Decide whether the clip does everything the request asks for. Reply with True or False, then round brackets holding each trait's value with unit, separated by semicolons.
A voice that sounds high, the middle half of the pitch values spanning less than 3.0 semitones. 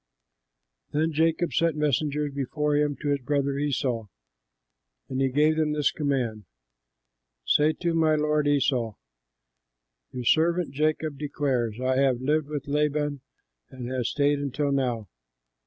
False (145 Hz; 2.4 semitones)